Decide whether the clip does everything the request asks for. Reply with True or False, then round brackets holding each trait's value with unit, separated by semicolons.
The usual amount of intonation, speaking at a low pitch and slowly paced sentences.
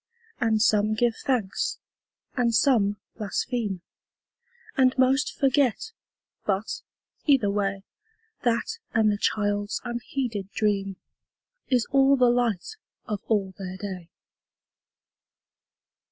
False (3.8 semitones; 220 Hz; 100 wpm)